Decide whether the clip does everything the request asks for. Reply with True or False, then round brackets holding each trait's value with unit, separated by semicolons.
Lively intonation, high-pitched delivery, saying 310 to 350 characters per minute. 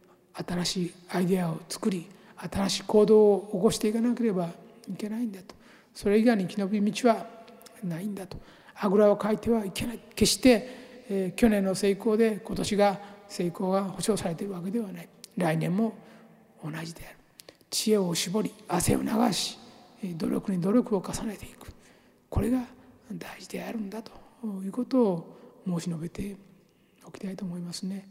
False (3.2 semitones; 205 Hz; 320 characters per minute)